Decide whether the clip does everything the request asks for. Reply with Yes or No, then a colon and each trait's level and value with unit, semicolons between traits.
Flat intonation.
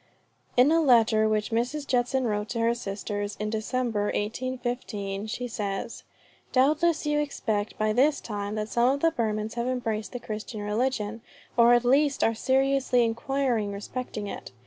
No: average, 3.3 semitones